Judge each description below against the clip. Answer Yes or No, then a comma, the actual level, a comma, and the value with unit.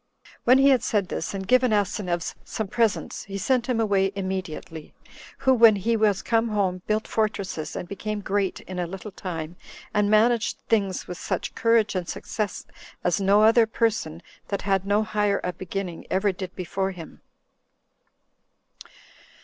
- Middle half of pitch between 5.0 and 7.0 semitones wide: No, average, 2.8 semitones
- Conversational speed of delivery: Yes, average, 160 wpm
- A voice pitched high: Yes, high, 200 Hz